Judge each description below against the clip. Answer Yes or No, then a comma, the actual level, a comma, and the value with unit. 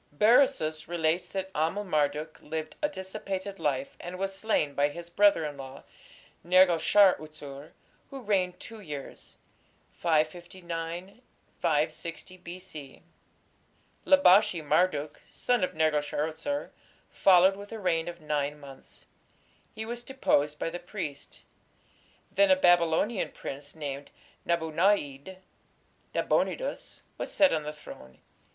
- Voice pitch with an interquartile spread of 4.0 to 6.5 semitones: Yes, average, 4.3 semitones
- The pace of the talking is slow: Yes, slow, 125 wpm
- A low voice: No, medium, 170 Hz